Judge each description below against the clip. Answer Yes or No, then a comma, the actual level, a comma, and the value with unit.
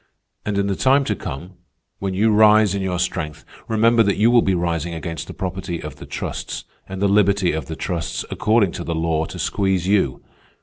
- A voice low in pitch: Yes, very low, 95 Hz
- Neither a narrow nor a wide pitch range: Yes, average, 3.7 semitones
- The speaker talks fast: Yes, fast, 210 wpm